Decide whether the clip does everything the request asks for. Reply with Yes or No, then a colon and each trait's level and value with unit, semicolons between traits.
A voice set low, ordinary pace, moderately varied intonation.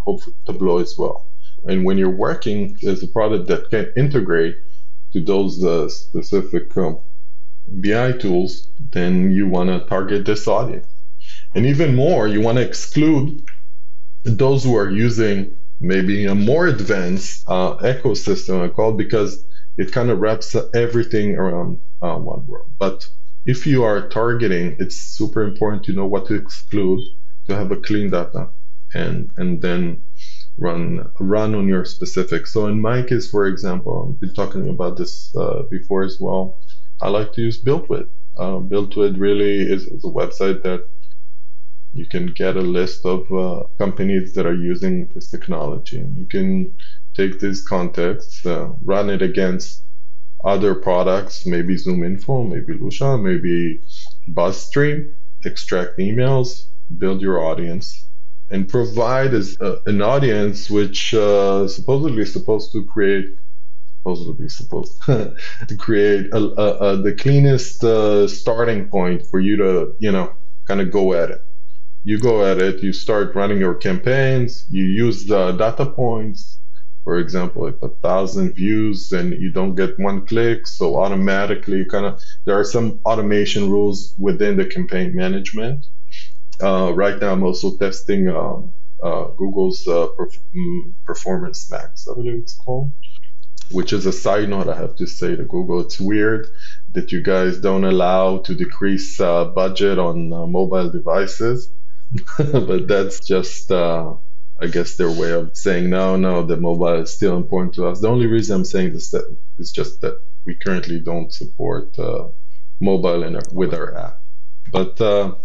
No: low, 105 Hz; average, 155 wpm; wide, 6.4 semitones